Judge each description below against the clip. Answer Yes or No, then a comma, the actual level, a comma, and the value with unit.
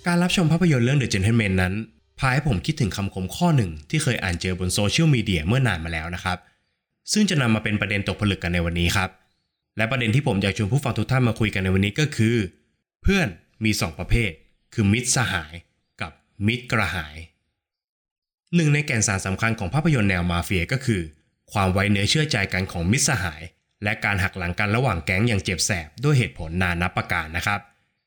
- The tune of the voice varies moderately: Yes, average, 5.0 semitones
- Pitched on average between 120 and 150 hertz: No, low, 105 Hz